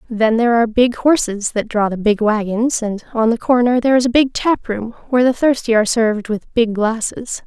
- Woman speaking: Yes, female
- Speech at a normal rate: No, fast, 215 wpm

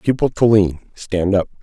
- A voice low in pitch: Yes, low, 100 Hz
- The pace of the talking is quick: No, average, 150 wpm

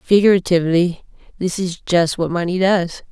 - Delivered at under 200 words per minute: Yes, slow, 135 wpm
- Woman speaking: Yes, female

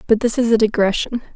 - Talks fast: Yes, fast, 220 wpm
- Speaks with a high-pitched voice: Yes, high, 220 Hz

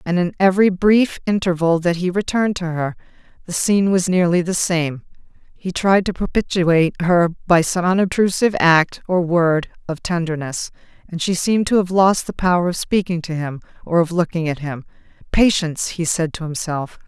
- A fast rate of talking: No, average, 180 wpm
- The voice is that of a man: No, female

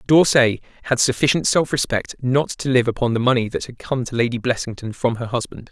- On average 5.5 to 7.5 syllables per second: Yes, 5.7 syllables/s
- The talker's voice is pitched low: Yes, low, 125 Hz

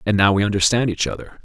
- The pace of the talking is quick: Yes, fast, 250 wpm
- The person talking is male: Yes, male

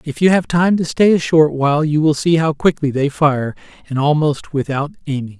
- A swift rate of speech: Yes, fast, 220 wpm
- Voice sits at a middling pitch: Yes, medium, 150 Hz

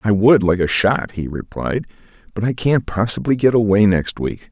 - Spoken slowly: No, average, 200 wpm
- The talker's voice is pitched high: No, low, 105 Hz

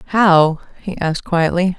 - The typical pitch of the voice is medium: Yes, medium, 175 Hz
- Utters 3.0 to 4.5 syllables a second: Yes, 3.9 syllables/s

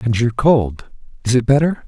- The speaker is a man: Yes, male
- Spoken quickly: No, average, 190 wpm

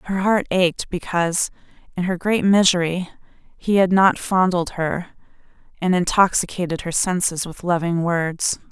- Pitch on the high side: No, medium, 180 Hz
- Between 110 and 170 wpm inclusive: Yes, average, 140 wpm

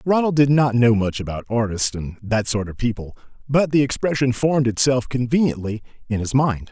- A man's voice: Yes, male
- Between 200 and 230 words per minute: No, average, 190 wpm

